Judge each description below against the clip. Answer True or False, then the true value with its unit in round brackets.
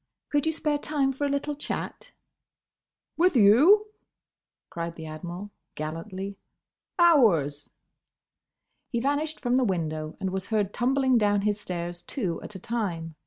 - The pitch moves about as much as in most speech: False (8.3 semitones)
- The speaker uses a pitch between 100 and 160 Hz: False (210 Hz)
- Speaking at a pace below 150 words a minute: True (140 wpm)